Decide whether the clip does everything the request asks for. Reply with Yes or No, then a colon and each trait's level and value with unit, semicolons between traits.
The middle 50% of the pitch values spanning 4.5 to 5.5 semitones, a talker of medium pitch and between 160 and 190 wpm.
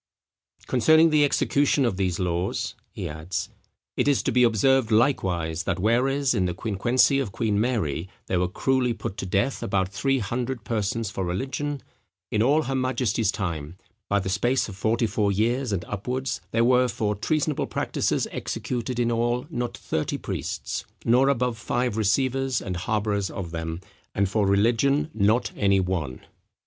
No: average, 4.9 semitones; low, 115 Hz; average, 165 wpm